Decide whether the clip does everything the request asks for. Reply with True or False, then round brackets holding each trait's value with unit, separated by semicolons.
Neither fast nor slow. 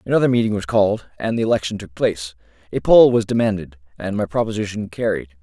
True (190 wpm)